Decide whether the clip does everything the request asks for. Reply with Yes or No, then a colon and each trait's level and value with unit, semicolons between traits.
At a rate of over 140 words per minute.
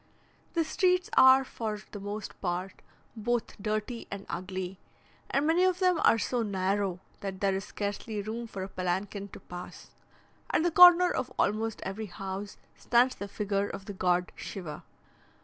Yes: average, 165 wpm